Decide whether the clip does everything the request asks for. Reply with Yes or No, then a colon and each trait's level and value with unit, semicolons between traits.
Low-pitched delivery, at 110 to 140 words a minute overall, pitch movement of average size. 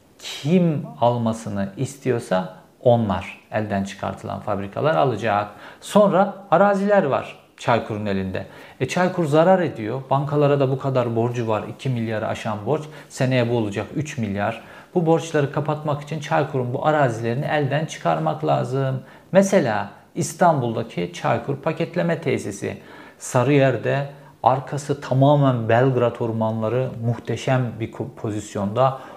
Yes: low, 130 Hz; average, 115 wpm; average, 4.9 semitones